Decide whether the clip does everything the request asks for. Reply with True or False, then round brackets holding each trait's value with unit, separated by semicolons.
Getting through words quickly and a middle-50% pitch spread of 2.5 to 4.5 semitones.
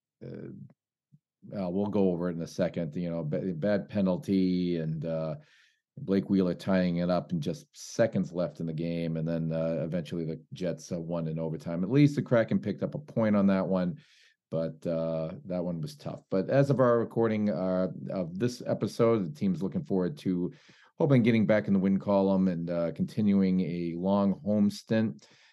False (195 wpm; 3.7 semitones)